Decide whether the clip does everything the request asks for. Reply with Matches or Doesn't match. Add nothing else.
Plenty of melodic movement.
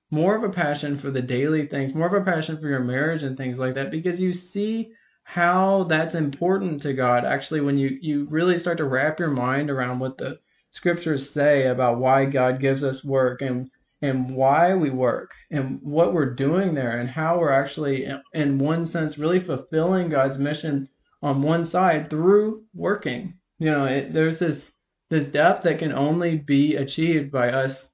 Doesn't match